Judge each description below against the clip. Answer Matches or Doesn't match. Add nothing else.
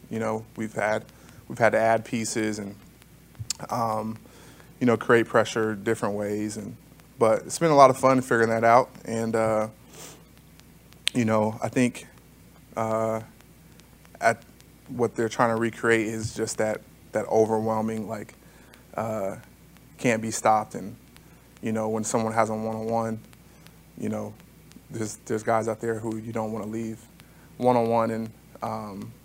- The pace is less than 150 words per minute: Doesn't match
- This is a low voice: Matches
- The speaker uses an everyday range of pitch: Doesn't match